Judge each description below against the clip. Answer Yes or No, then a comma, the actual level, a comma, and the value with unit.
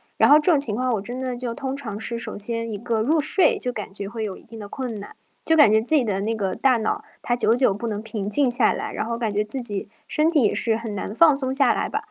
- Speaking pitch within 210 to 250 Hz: Yes, high, 235 Hz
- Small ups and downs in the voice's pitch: No, average, 3.8 semitones